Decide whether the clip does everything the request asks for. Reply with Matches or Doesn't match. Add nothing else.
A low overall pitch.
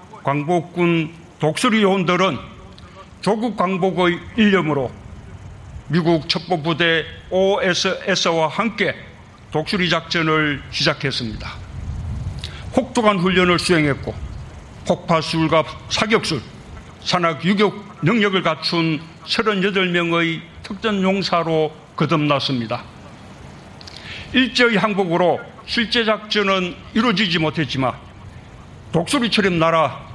Doesn't match